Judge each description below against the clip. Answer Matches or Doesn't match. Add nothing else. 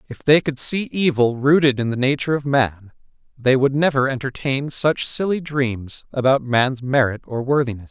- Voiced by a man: Matches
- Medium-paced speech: Matches